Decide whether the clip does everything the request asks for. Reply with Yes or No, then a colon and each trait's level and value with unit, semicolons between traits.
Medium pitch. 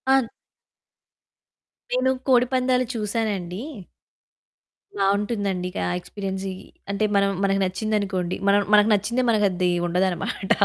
No: high, 200 Hz